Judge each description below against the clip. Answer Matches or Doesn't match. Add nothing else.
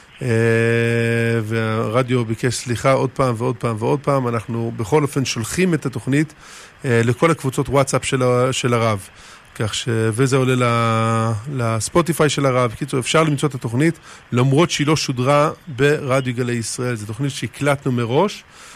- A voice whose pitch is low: Matches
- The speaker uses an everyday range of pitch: Matches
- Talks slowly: Doesn't match